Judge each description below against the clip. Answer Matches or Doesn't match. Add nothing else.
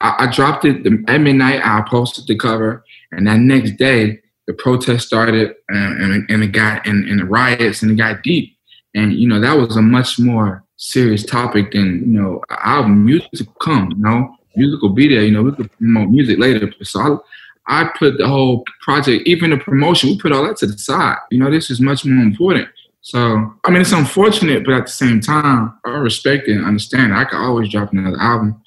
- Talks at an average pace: Doesn't match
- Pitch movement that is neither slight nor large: Matches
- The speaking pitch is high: Doesn't match